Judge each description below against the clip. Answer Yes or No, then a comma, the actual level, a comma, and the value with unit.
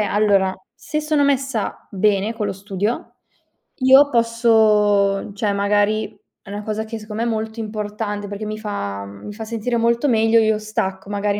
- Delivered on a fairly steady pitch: Yes, narrow, 2.0 semitones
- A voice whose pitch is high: Yes, high, 215 Hz